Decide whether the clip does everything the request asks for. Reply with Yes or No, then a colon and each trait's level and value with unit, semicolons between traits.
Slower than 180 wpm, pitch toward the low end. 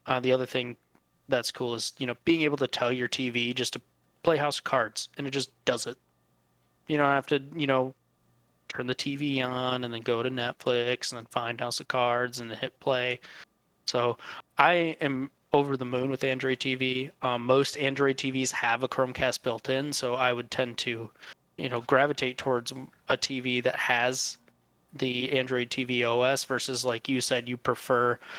No: average, 195 wpm; low, 130 Hz